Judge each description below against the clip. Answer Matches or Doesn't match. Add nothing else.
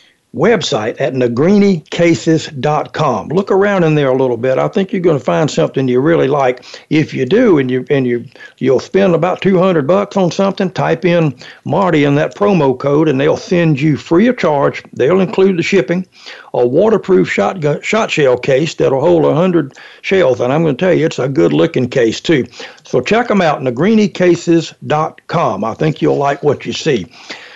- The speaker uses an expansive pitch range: Doesn't match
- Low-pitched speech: Doesn't match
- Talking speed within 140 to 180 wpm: Doesn't match